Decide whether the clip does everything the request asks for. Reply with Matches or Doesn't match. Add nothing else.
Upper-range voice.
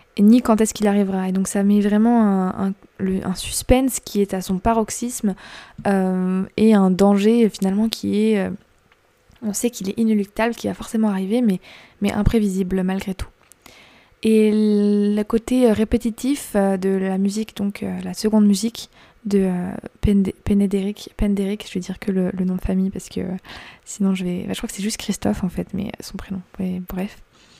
Matches